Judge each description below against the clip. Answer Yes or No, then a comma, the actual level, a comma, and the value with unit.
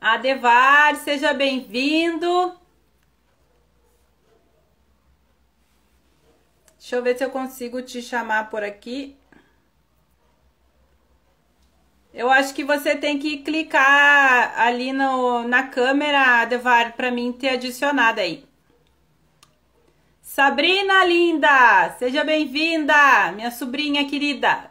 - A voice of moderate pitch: No, very high, 250 Hz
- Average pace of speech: No, slow, 90 wpm